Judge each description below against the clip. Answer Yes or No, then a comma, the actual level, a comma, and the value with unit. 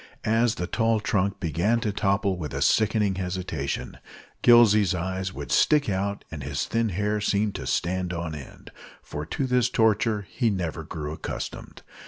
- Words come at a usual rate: Yes, average, 165 wpm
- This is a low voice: Yes, low, 100 Hz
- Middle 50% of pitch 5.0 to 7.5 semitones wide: No, average, 3.8 semitones